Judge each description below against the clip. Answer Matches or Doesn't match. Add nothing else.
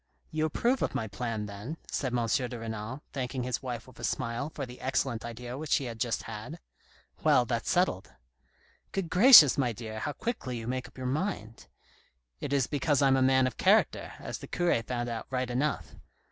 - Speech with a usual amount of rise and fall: Matches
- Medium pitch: Doesn't match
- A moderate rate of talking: Doesn't match